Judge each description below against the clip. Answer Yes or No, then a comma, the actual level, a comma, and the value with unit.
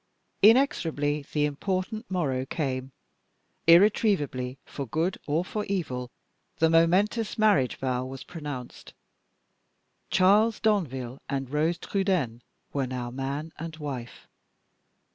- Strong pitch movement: Yes, wide, 6.2 semitones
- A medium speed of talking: No, slow, 105 wpm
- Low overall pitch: No, medium, 150 Hz